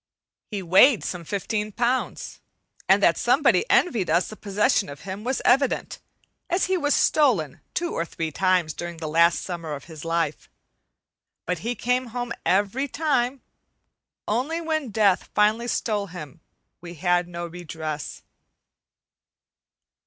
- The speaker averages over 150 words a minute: No, average, 140 wpm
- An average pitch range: No, wide, 6.5 semitones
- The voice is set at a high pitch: Yes, high, 200 Hz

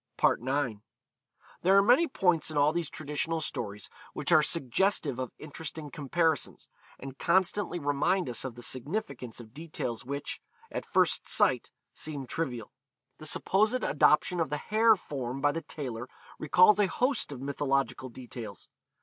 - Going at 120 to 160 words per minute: Yes, average, 150 wpm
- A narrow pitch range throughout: No, average, 5.0 semitones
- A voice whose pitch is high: No, medium, 145 Hz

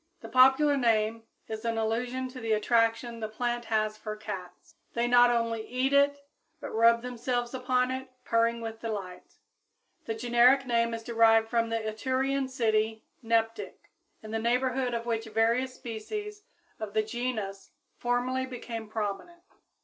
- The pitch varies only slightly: Yes, narrow, 2.2 semitones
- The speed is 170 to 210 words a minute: No, average, 150 wpm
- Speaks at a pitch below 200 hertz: No, high, 230 Hz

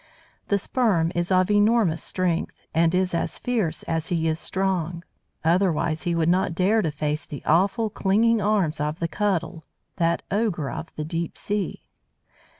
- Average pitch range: Yes, average, 3.6 semitones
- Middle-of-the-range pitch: Yes, medium, 175 Hz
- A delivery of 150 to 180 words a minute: Yes, average, 160 wpm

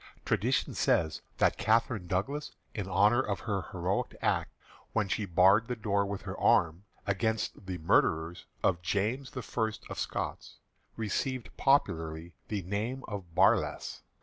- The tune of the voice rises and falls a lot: No, average, 3.9 semitones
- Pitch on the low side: Yes, low, 100 Hz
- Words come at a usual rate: Yes, average, 145 wpm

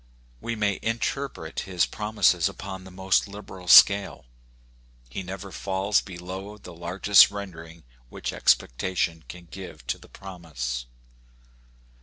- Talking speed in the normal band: No, slow, 120 wpm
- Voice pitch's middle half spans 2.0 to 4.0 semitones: Yes, average, 2.9 semitones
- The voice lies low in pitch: Yes, very low, 95 Hz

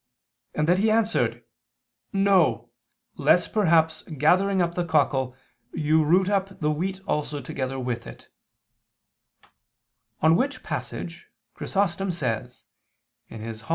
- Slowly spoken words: Yes, slow, 115 wpm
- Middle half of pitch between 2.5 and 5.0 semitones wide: No, wide, 5.5 semitones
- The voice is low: No, medium, 160 Hz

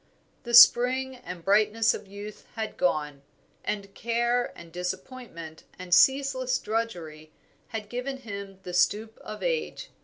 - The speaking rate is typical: No, slow, 130 wpm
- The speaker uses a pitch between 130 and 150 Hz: No, high, 215 Hz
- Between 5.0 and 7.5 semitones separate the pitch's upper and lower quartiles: Yes, average, 5.3 semitones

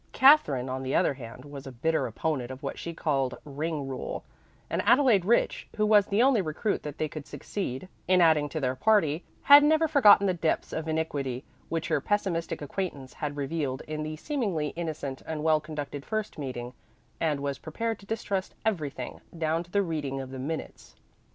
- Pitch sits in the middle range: Yes, medium, 155 Hz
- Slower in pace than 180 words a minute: No, average, 190 wpm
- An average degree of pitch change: No, wide, 5.8 semitones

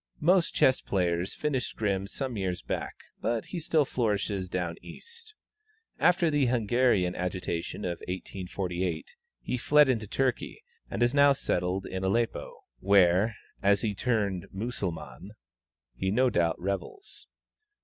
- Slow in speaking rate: Yes, slow, 130 wpm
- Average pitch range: No, wide, 5.8 semitones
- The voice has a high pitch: No, low, 100 Hz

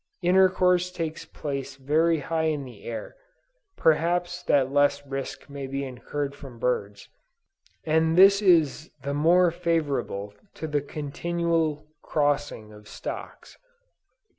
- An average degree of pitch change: Yes, average, 3.6 semitones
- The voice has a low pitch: No, medium, 150 Hz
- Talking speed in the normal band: No, slow, 120 wpm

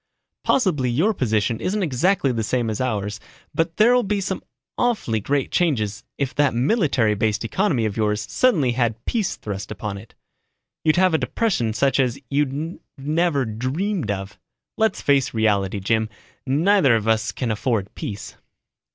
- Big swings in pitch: Yes, wide, 7.4 semitones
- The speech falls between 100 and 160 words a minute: Yes, average, 155 wpm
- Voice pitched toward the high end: No, low, 130 Hz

